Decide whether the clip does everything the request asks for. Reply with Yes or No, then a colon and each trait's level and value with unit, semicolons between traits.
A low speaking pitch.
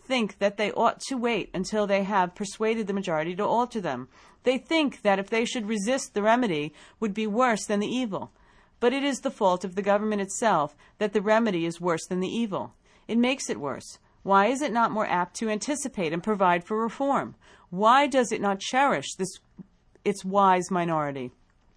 No: high, 210 Hz